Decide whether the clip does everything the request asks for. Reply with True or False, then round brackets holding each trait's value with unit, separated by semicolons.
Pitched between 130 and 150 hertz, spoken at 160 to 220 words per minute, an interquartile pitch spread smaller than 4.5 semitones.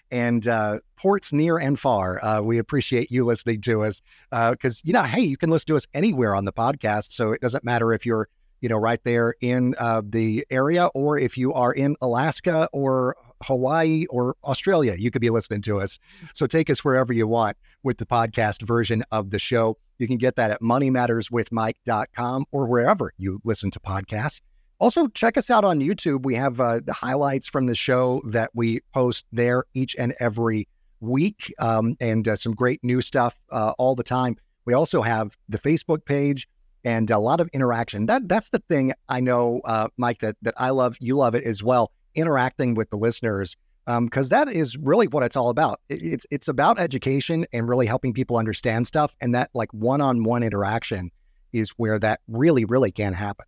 False (120 Hz; 200 wpm; 3.2 semitones)